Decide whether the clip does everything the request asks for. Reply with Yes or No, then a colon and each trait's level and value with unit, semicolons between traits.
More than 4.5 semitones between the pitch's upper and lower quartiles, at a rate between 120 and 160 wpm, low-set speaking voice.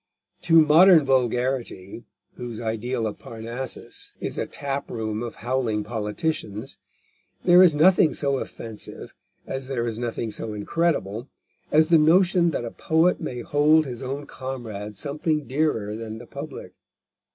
Yes: average, 5.2 semitones; average, 140 wpm; low, 130 Hz